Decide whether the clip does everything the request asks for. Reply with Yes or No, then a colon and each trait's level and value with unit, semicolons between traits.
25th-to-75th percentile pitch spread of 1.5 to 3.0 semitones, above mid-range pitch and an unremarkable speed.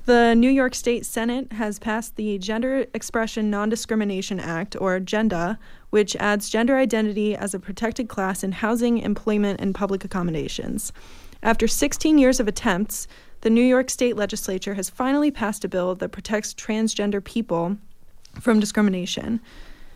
Yes: narrow, 2.6 semitones; high, 215 Hz; average, 150 wpm